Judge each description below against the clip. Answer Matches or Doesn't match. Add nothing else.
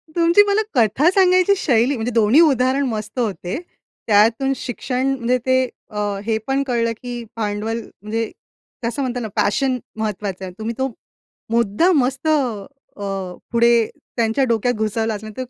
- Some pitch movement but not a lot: Matches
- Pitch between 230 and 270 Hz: Matches